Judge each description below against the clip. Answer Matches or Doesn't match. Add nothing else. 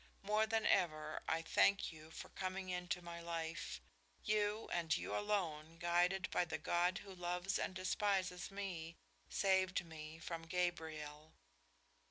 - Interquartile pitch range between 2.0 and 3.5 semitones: Matches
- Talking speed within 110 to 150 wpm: Matches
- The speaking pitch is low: Doesn't match